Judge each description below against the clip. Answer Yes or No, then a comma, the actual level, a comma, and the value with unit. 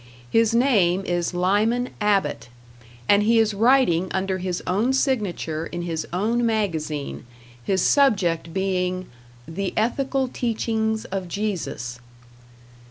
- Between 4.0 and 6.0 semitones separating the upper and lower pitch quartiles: Yes, average, 4.3 semitones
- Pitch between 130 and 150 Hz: No, high, 195 Hz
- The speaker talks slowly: Yes, slow, 115 wpm